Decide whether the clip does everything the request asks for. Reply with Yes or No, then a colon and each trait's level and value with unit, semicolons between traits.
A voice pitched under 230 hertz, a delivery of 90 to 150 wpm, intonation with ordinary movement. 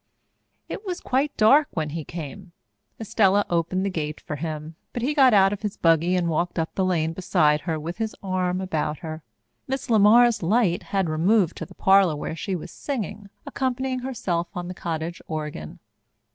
No: medium, 185 Hz; average, 185 wpm; average, 5.0 semitones